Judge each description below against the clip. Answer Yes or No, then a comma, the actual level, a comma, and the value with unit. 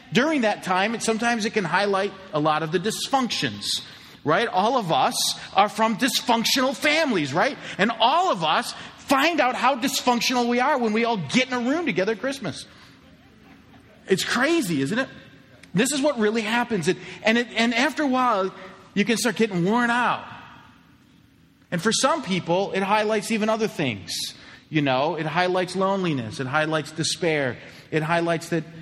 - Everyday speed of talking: Yes, average, 180 wpm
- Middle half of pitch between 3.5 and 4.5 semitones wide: No, wide, 5.6 semitones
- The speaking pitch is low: No, high, 210 Hz